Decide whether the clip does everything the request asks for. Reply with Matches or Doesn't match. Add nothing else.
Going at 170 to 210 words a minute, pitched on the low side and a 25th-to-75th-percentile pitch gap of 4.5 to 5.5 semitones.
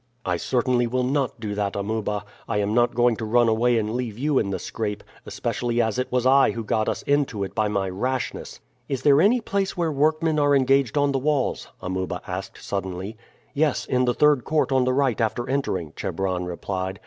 Matches